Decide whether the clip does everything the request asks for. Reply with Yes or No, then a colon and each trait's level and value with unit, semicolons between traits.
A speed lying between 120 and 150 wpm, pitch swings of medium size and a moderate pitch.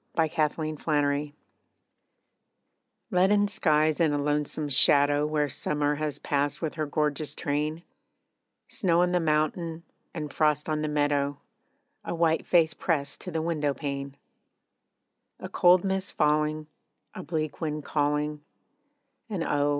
No: slow, 135 wpm; narrow, 1.9 semitones; medium, 150 Hz